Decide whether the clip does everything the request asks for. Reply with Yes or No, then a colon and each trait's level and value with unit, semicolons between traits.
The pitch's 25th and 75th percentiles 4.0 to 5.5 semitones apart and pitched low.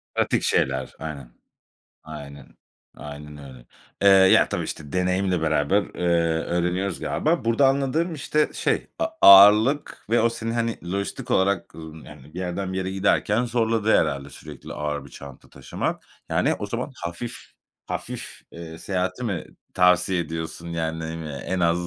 Yes: average, 5.1 semitones; very low, 90 Hz